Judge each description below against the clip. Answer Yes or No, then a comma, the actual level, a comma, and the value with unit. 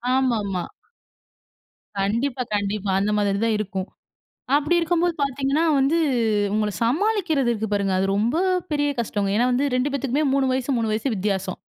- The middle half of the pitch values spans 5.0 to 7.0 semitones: Yes, wide, 5.5 semitones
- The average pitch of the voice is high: Yes, high, 240 Hz